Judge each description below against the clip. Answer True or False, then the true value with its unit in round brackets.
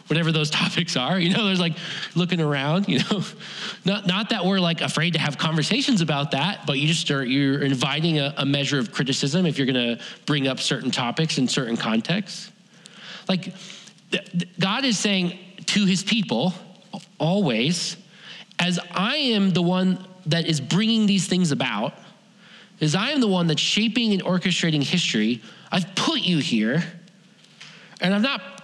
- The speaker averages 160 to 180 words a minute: True (170 wpm)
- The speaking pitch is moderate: True (180 Hz)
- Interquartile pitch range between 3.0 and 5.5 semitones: True (4.1 semitones)